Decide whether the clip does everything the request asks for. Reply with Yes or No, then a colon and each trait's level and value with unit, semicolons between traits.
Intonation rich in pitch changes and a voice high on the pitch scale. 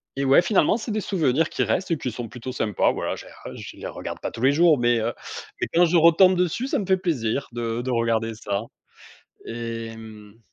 No: wide, 7.1 semitones; low, 130 Hz